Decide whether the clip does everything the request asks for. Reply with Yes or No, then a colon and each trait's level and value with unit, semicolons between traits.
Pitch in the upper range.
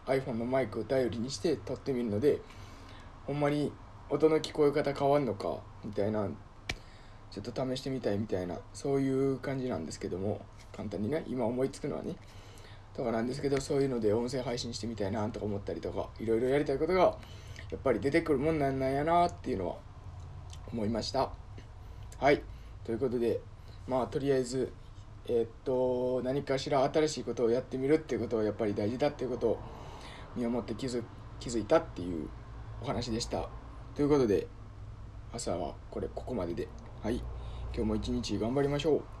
No: low, 115 Hz